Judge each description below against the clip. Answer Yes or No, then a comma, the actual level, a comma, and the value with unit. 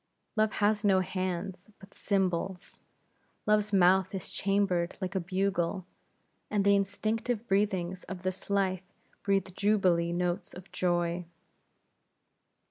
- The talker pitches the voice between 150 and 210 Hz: Yes, high, 190 Hz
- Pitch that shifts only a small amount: Yes, narrow, 2.1 semitones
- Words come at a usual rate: No, slow, 120 wpm